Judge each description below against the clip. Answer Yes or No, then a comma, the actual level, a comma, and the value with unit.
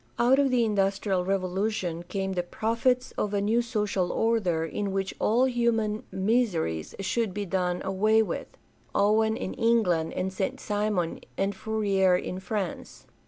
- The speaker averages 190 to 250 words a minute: No, average, 155 wpm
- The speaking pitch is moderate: No, high, 205 Hz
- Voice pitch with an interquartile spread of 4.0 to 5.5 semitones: No, average, 3.0 semitones